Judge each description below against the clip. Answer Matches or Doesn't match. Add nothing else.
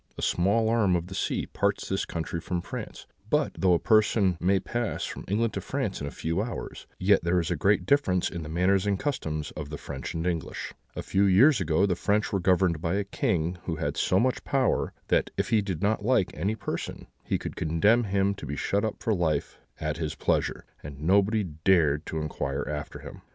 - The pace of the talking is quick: Matches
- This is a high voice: Doesn't match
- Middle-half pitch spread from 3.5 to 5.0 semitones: Matches